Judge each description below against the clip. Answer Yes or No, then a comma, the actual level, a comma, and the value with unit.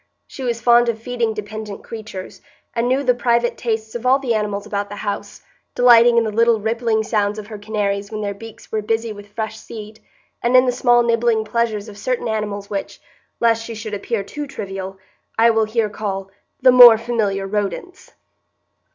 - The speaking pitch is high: Yes, high, 220 Hz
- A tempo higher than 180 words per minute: Yes, average, 190 wpm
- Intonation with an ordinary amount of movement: No, narrow, 2.3 semitones